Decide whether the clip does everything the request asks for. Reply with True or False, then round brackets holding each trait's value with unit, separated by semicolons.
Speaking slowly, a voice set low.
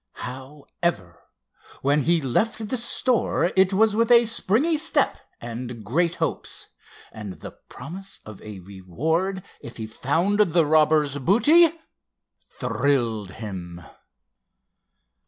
False (110 wpm; 150 Hz)